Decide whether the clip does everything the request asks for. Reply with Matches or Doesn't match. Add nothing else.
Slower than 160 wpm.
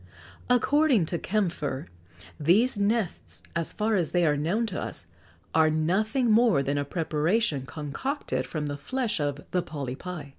Matches